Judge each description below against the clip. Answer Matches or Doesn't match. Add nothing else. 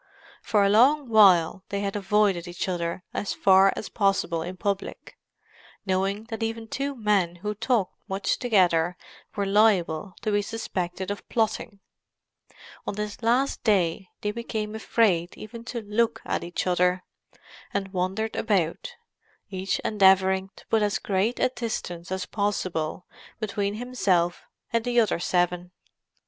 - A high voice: Matches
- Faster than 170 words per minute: Doesn't match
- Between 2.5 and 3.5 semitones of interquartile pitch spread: Matches